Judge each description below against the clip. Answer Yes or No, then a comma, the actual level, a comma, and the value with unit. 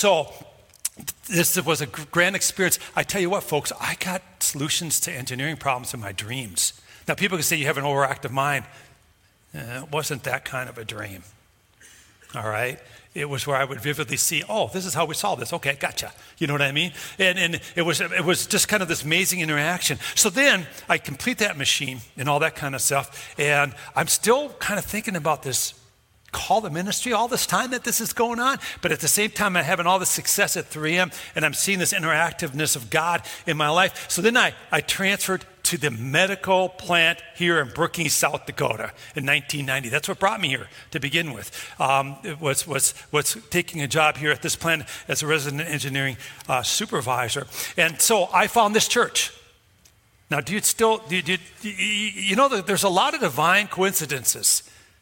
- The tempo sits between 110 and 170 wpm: No, fast, 205 wpm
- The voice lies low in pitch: No, medium, 155 Hz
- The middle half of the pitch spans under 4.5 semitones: No, average, 5.1 semitones